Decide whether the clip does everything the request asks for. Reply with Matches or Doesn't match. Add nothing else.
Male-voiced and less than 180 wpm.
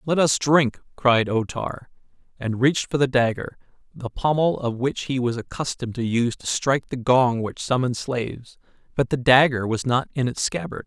Doesn't match